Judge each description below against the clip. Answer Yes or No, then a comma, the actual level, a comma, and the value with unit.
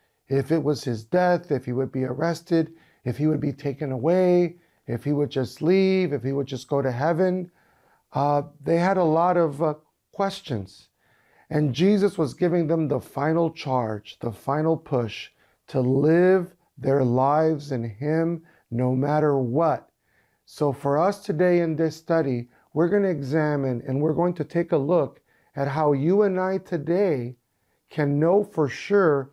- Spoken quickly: No, average, 170 wpm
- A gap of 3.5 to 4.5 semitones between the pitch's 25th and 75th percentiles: Yes, average, 4.1 semitones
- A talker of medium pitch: Yes, medium, 155 Hz